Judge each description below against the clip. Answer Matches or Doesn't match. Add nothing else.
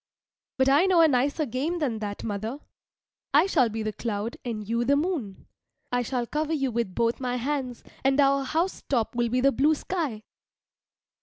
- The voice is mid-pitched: Doesn't match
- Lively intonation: Doesn't match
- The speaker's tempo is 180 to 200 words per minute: Matches